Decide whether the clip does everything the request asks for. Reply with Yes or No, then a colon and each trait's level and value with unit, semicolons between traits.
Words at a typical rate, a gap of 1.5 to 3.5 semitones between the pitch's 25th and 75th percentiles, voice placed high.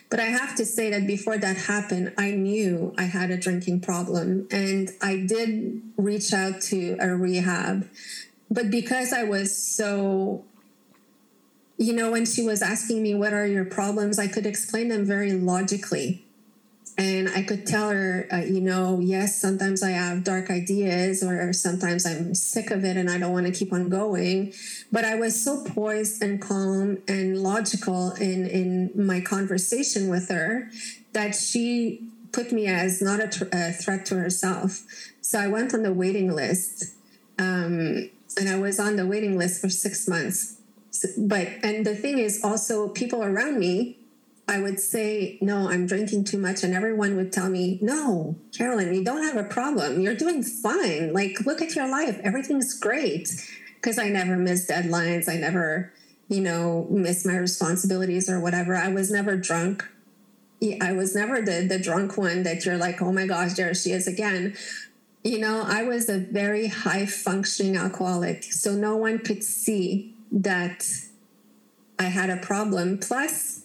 Yes: average, 175 wpm; average, 2.7 semitones; high, 195 Hz